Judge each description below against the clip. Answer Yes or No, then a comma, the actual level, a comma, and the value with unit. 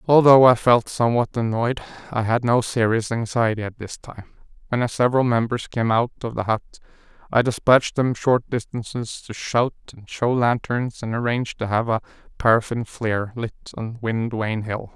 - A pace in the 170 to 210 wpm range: Yes, average, 175 wpm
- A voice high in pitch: No, low, 115 Hz